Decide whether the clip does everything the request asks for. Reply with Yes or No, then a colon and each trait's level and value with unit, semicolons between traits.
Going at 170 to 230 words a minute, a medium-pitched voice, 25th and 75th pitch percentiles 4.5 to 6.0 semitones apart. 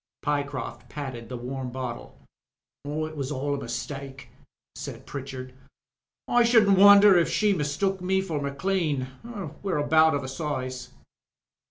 No: slow, 135 wpm; medium, 145 Hz; wide, 5.5 semitones